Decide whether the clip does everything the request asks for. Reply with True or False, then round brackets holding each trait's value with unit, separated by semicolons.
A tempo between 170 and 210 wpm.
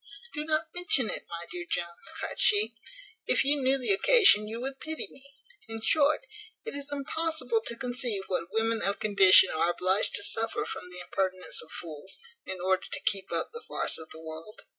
True (200 wpm)